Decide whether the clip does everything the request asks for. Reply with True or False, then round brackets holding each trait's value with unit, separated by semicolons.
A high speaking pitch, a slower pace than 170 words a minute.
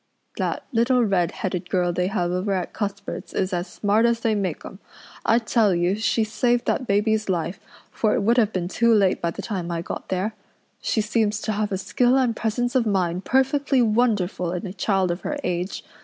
False (205 Hz; 205 wpm)